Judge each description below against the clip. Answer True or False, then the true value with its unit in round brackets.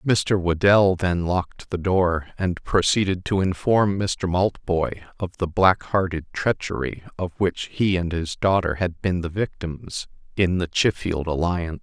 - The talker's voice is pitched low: True (90 Hz)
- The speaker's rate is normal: True (155 wpm)